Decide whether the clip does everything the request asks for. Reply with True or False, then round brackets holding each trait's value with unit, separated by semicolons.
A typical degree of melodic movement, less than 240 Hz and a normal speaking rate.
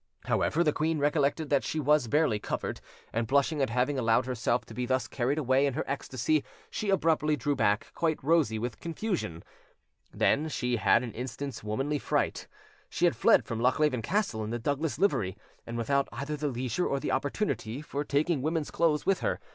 True (4.1 semitones; 140 Hz; 190 wpm)